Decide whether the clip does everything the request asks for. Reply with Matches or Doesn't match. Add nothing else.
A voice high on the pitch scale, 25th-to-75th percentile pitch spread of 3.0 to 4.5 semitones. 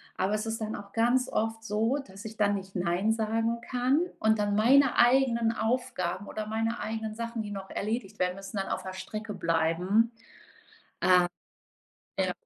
Doesn't match